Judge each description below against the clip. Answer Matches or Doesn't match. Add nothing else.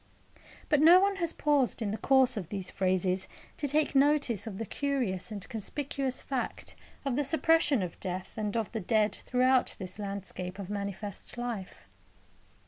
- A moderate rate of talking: Matches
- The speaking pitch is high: Matches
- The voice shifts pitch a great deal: Matches